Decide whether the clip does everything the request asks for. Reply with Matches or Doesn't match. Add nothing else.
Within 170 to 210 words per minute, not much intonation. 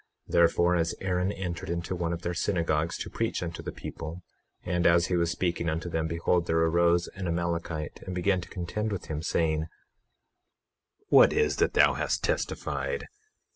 Matches